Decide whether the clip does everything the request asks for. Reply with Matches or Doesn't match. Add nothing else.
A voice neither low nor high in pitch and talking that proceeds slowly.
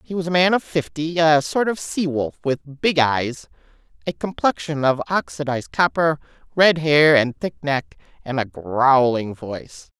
Doesn't match